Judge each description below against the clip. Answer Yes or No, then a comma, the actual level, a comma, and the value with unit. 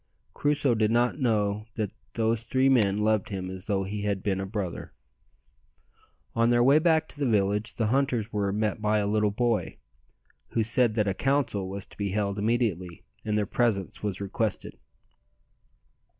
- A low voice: Yes, low, 105 Hz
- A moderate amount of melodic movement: Yes, average, 3.0 semitones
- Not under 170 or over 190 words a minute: Yes, average, 175 wpm